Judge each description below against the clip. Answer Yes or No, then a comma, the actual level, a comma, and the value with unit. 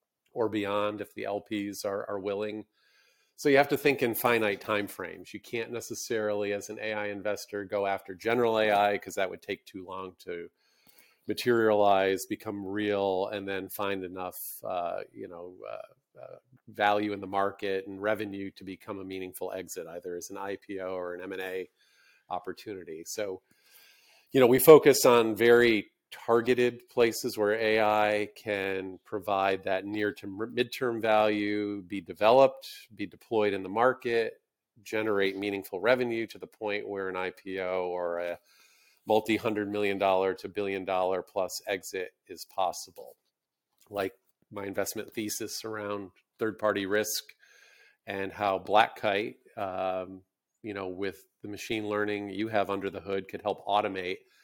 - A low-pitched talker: Yes, low, 105 Hz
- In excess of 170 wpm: No, average, 155 wpm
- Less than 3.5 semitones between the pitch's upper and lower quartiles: Yes, average, 2.8 semitones